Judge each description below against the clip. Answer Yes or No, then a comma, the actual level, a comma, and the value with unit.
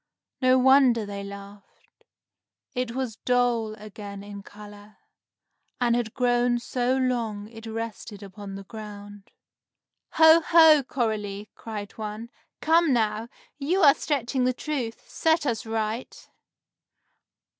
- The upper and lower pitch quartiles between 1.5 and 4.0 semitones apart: Yes, average, 3.6 semitones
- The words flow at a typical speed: No, slow, 120 wpm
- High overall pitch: Yes, high, 230 Hz